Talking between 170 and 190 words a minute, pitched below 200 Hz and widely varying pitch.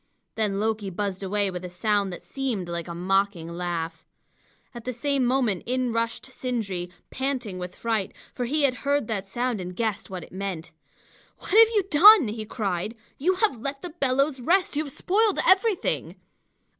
No: average, 180 wpm; high, 225 Hz; wide, 6.2 semitones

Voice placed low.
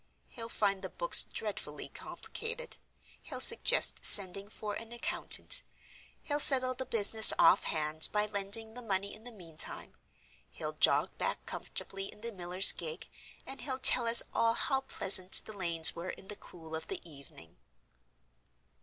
No: high, 210 Hz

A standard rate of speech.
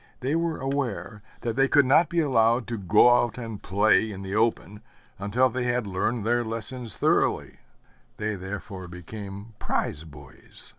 Yes: average, 160 wpm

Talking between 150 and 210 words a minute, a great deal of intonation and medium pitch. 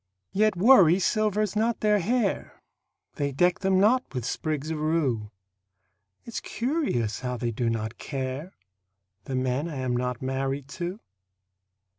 No: average, 140 wpm; wide, 8.2 semitones; medium, 155 Hz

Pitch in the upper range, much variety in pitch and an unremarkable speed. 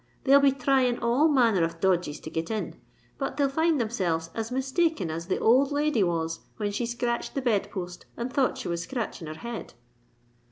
Yes: high, 235 Hz; wide, 7.2 semitones; average, 195 wpm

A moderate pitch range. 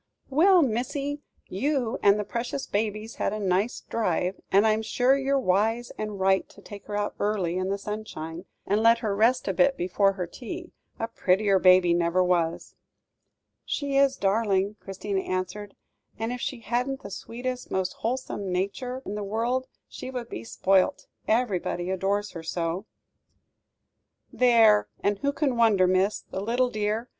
Yes: average, 4.3 semitones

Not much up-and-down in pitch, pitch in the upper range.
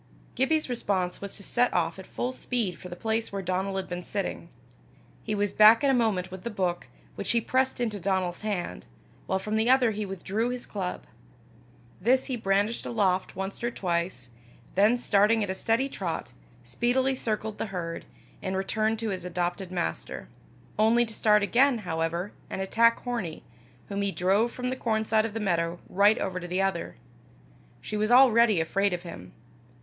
No: average, 3.9 semitones; high, 205 Hz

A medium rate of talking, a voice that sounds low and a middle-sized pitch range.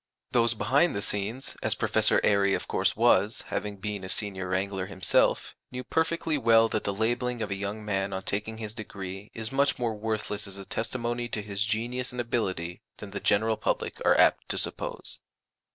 Yes: average, 190 wpm; low, 105 Hz; average, 3.0 semitones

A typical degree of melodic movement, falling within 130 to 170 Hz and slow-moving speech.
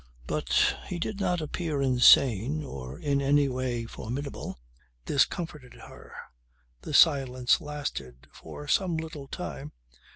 Yes: average, 3.8 semitones; medium, 140 Hz; slow, 130 wpm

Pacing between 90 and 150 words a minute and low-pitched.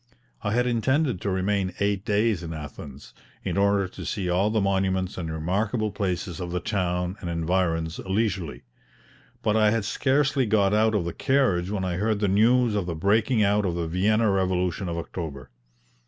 No: average, 185 wpm; low, 100 Hz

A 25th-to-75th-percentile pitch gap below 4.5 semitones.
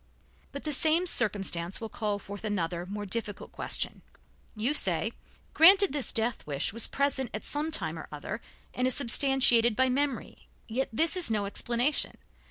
No: wide, 5.4 semitones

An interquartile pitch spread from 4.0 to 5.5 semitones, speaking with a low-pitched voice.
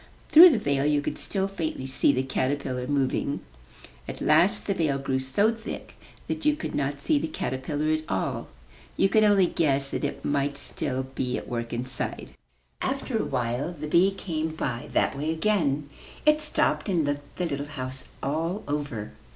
No: average, 4.4 semitones; medium, 145 Hz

